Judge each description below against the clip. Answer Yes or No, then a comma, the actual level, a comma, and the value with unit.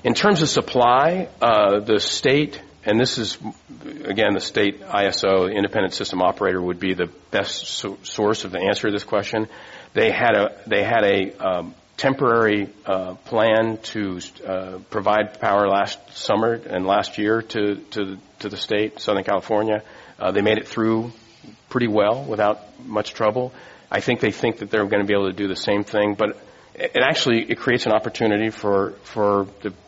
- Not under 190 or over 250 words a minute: No, average, 180 wpm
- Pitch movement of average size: No, narrow, 1.9 semitones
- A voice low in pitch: Yes, low, 105 Hz